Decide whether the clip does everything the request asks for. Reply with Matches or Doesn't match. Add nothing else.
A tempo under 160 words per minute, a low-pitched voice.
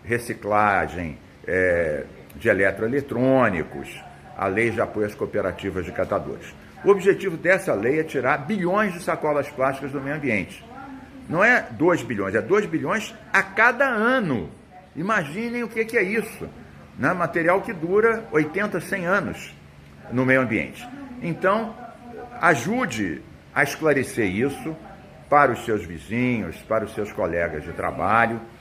Doesn't match